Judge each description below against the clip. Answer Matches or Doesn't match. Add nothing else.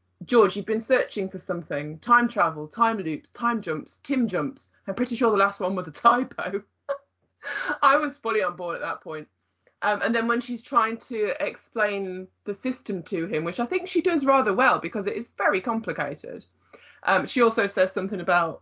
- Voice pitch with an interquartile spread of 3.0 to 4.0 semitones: Doesn't match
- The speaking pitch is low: Doesn't match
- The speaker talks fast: Doesn't match